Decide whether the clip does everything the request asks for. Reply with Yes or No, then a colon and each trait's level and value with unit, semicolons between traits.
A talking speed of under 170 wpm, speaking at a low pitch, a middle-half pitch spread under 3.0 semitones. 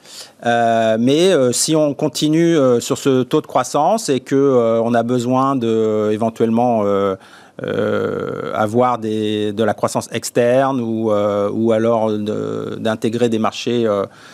Yes: slow, 145 wpm; low, 115 Hz; narrow, 2.6 semitones